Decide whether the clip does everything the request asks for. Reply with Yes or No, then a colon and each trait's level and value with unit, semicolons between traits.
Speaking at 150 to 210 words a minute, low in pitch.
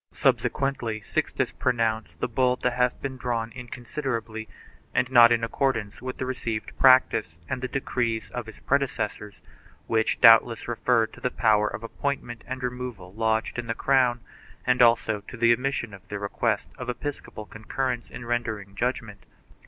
Yes: average, 165 wpm; low, 120 Hz